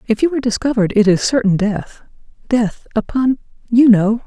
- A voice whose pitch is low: No, high, 230 Hz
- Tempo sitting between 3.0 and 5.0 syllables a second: No, 5.5 syllables/s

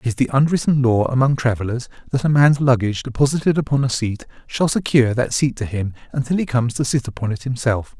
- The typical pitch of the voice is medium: No, low, 125 Hz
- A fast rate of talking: Yes, fast, 220 wpm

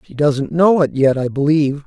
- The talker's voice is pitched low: No, medium, 145 Hz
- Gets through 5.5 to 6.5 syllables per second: No, 5.2 syllables/s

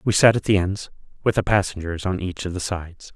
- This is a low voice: Yes, very low, 95 Hz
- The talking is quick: Yes, fast, 245 wpm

